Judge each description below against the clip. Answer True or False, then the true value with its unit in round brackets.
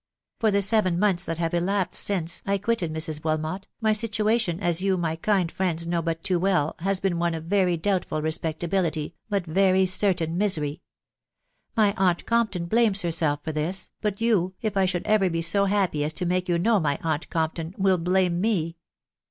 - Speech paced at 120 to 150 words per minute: False (190 wpm)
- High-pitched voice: False (180 Hz)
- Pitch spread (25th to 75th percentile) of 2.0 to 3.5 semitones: True (3.1 semitones)